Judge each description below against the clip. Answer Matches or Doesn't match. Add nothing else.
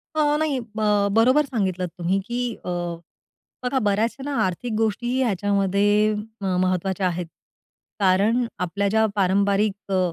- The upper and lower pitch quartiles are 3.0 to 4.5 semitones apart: Matches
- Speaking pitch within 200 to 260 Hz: Matches